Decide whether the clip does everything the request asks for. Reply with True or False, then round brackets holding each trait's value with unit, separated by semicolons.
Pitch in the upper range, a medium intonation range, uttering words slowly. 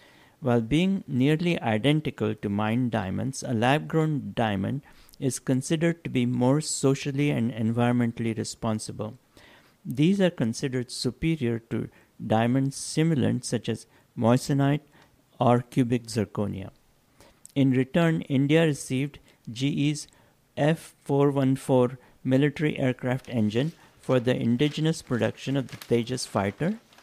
False (130 Hz; 3.7 semitones; 110 wpm)